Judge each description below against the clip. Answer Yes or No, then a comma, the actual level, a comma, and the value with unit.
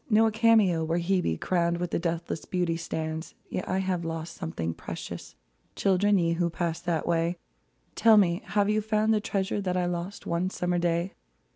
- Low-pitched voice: No, medium, 175 Hz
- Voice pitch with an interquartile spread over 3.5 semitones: No, average, 2.7 semitones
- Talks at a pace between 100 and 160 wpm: No, average, 185 wpm